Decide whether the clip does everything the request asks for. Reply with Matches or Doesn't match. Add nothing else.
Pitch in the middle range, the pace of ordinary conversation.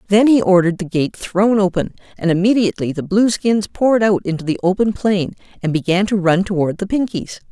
Doesn't match